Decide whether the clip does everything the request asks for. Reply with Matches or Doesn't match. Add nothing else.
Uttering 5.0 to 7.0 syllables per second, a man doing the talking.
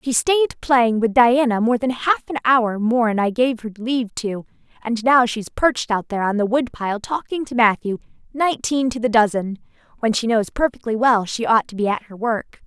Doesn't match